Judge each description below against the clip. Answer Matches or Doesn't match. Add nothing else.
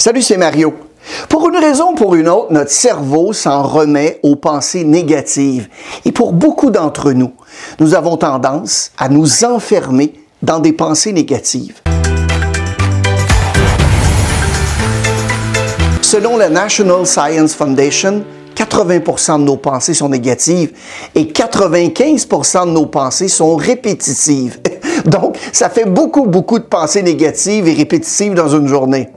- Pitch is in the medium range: Matches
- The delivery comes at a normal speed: Doesn't match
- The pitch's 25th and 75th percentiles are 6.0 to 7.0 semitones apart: Matches